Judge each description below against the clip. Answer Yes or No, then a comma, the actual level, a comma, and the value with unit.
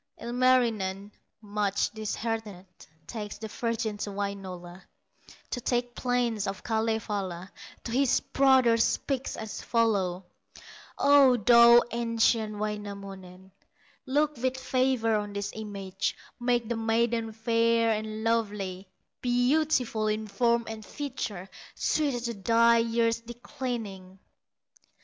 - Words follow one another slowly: Yes, slow, 110 wpm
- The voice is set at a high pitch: Yes, high, 225 Hz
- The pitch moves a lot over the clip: No, average, 2.8 semitones